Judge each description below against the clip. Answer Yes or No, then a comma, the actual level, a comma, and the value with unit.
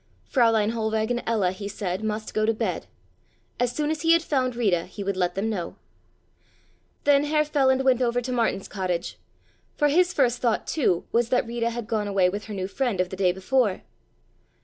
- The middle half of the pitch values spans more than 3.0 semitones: Yes, average, 4.5 semitones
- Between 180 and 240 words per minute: Yes, average, 200 wpm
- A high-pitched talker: Yes, high, 225 Hz